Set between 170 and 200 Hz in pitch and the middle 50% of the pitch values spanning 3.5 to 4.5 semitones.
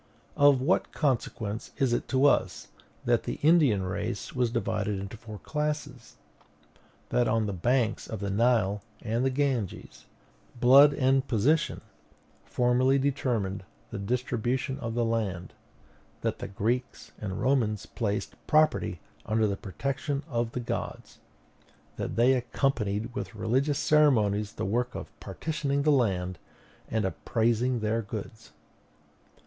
No: low, 120 Hz; average, 4.0 semitones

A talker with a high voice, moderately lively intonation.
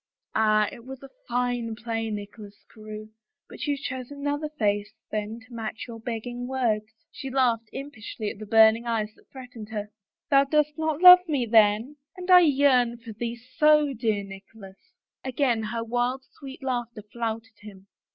Yes: high, 235 Hz; average, 3.7 semitones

